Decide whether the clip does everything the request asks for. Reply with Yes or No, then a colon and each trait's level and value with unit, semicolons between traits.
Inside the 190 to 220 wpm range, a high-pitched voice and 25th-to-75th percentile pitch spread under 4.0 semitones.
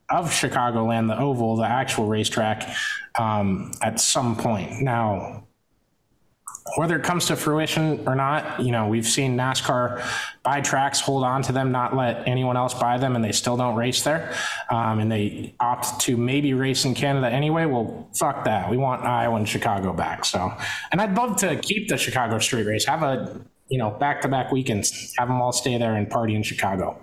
No: average, 200 wpm; low, 125 Hz; average, 2.9 semitones